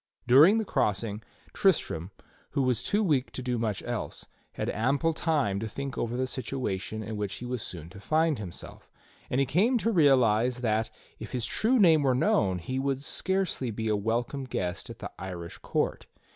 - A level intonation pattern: No, average, 5.1 semitones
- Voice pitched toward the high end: No, low, 125 Hz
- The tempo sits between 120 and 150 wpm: No, average, 190 wpm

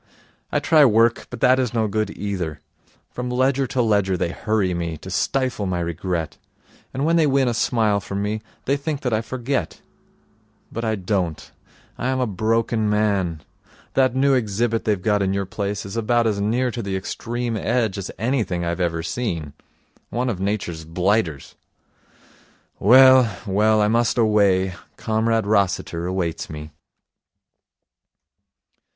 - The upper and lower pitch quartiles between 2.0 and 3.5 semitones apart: No, average, 4.3 semitones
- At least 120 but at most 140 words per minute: No, average, 155 wpm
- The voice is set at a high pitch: No, low, 110 Hz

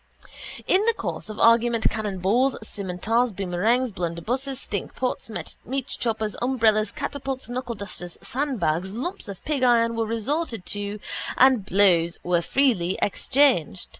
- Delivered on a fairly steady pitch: No, average, 4.8 semitones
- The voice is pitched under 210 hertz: No, high, 225 Hz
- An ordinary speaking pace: No, slow, 120 wpm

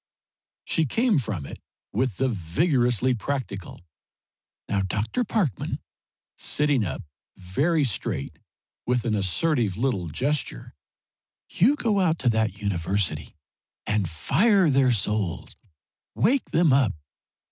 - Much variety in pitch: Yes, wide, 7.4 semitones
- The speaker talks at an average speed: No, slow, 115 wpm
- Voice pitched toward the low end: Yes, low, 120 Hz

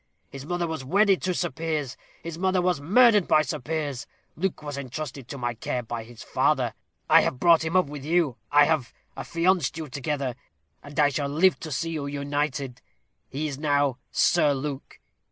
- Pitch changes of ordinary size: Yes, average, 3.4 semitones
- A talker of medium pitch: Yes, medium, 150 Hz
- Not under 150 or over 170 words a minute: No, average, 190 wpm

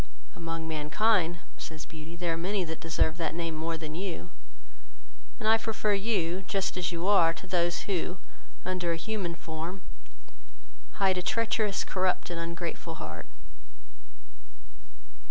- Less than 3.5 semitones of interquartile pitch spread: Yes, average, 2.7 semitones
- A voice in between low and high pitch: Yes, medium, 175 Hz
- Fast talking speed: No, average, 140 wpm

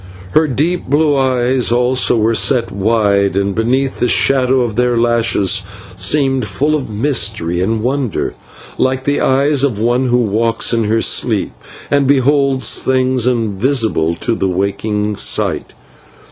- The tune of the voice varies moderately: Yes, average, 3.7 semitones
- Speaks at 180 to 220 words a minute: No, average, 145 wpm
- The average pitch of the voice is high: No, low, 120 Hz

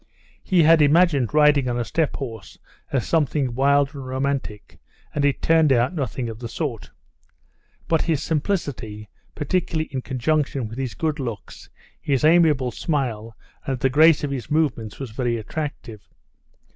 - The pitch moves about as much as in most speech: Yes, average, 4.2 semitones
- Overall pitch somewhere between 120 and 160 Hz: Yes, medium, 140 Hz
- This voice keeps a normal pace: Yes, average, 155 wpm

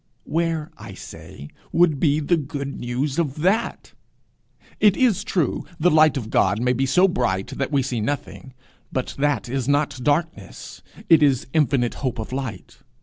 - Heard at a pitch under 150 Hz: Yes, medium, 140 Hz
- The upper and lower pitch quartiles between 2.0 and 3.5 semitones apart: No, average, 3.9 semitones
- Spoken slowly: No, average, 165 wpm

